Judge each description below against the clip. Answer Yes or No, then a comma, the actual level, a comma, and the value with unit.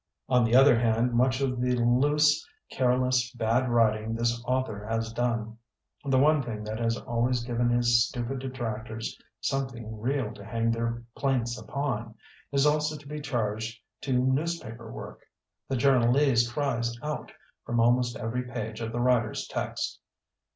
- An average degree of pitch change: No, narrow, 2.3 semitones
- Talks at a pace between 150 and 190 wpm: Yes, average, 160 wpm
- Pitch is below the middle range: Yes, low, 120 Hz